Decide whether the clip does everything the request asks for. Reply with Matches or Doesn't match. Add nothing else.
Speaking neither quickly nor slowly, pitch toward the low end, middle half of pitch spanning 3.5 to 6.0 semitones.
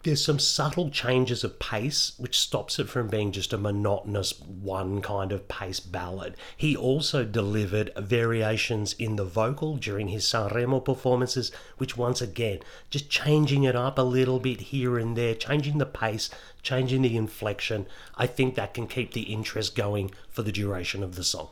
Matches